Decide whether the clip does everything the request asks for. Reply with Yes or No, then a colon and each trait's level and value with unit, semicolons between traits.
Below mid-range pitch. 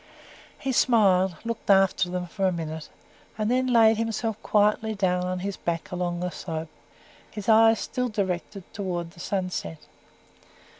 No: high, 195 Hz